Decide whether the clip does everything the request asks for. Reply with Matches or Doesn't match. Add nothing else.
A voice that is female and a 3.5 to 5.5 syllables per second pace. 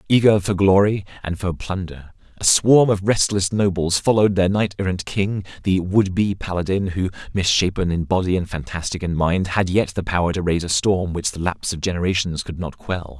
Doesn't match